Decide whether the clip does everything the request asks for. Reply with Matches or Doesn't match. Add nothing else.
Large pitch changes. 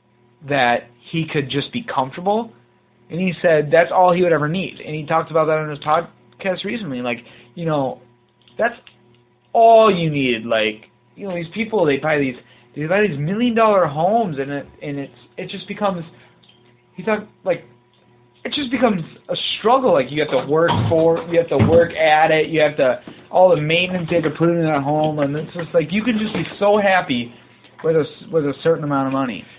Matches